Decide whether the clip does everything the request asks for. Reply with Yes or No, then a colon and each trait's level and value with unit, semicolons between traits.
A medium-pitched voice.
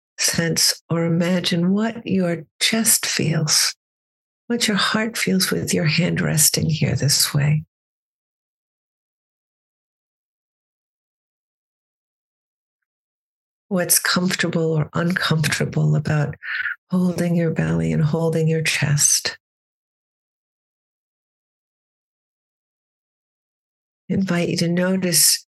Yes: medium, 170 Hz